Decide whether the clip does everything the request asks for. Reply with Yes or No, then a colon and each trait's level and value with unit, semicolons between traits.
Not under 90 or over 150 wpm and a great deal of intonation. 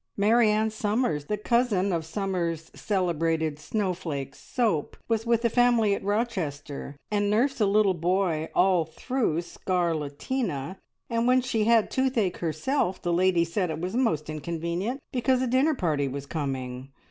Yes: average, 145 wpm; wide, 6.1 semitones